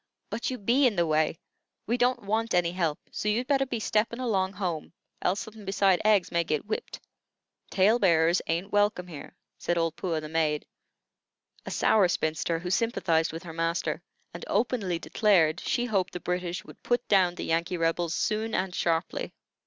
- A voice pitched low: No, medium, 185 Hz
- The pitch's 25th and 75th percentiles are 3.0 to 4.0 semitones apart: No, average, 4.4 semitones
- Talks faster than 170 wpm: Yes, average, 180 wpm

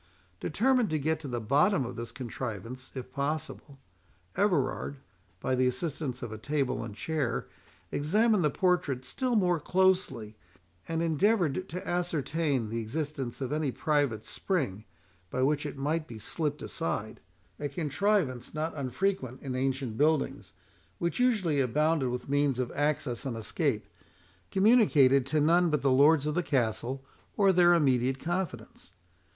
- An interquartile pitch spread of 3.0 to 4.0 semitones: No, average, 4.7 semitones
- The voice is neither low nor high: Yes, medium, 145 Hz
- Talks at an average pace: Yes, average, 145 wpm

